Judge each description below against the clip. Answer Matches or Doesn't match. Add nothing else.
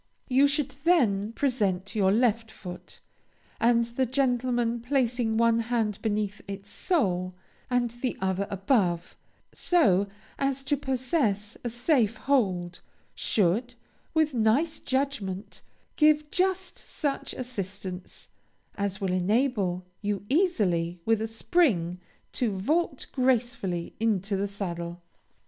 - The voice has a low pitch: Doesn't match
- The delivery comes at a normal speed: Doesn't match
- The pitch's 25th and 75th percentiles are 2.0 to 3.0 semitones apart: Doesn't match